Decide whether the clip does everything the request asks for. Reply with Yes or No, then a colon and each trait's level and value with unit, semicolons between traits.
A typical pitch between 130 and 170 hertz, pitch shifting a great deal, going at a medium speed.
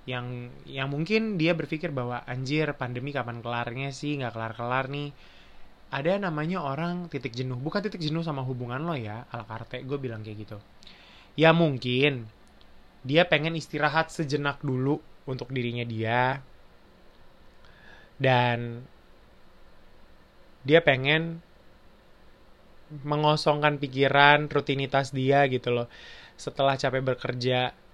No: low, 135 Hz; average, 3.5 semitones; average, 120 wpm